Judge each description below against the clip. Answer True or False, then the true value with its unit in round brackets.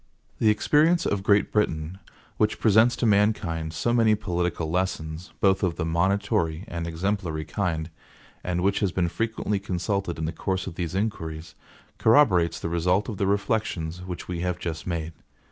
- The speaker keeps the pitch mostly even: False (3.7 semitones)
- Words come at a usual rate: True (165 wpm)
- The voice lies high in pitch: False (90 Hz)